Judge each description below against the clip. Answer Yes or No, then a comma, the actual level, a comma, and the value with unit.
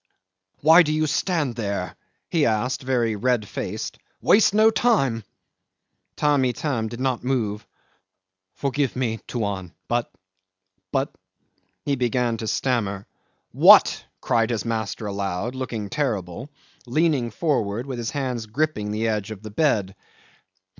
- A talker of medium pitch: No, low, 120 Hz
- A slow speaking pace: Yes, slow, 130 wpm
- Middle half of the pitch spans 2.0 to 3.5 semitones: No, average, 4.4 semitones